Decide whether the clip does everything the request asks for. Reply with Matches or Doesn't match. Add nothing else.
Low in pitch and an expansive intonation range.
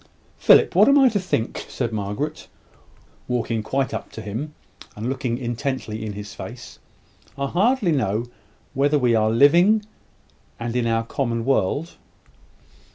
Doesn't match